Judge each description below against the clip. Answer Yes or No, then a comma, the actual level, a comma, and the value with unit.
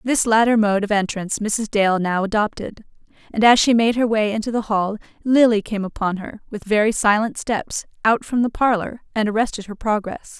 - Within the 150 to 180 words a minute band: No, average, 195 wpm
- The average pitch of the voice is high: Yes, high, 215 Hz